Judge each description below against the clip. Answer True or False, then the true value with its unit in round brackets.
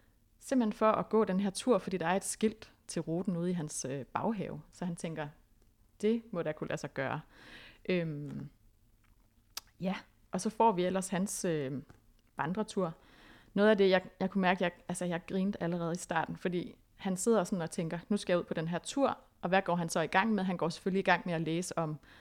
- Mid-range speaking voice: True (180 Hz)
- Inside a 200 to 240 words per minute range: True (225 wpm)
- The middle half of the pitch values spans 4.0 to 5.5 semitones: False (3.5 semitones)